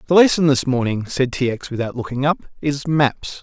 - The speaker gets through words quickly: Yes, fast, 210 wpm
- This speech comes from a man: Yes, male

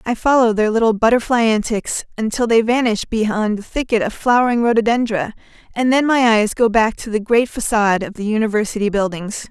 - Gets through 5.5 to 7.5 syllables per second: Yes, 5.6 syllables/s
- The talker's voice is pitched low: No, high, 220 Hz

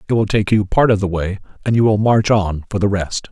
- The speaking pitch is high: No, low, 100 Hz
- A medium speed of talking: No, fast, 290 wpm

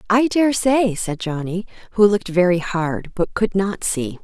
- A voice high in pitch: Yes, high, 195 Hz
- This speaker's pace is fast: No, average, 170 wpm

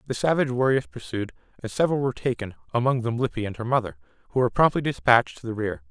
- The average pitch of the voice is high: No, low, 120 Hz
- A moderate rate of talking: No, fast, 215 wpm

